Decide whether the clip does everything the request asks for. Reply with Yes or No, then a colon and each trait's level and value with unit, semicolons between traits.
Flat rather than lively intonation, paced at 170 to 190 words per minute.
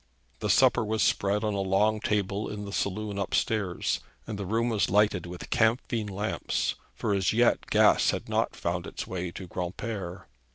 Yes: narrow, 2.1 semitones; average, 180 wpm